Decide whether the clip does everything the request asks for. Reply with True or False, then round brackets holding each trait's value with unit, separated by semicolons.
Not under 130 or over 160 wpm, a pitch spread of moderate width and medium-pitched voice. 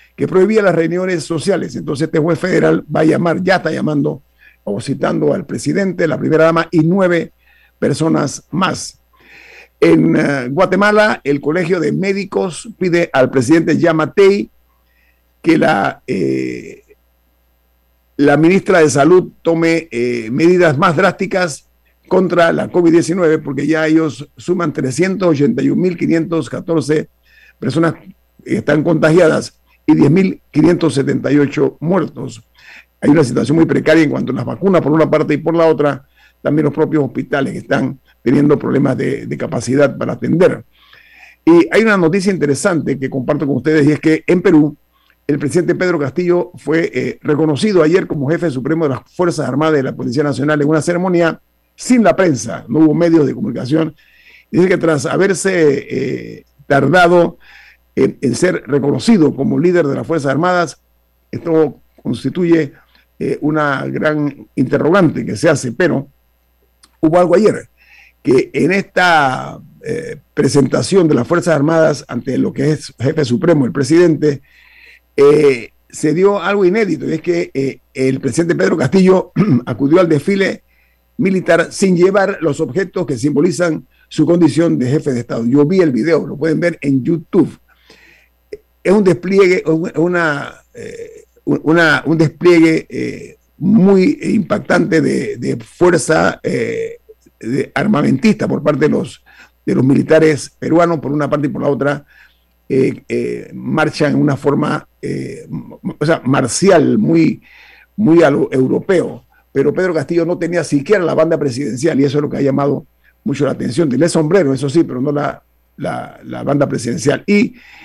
True (150 wpm; 3.8 semitones; 160 Hz)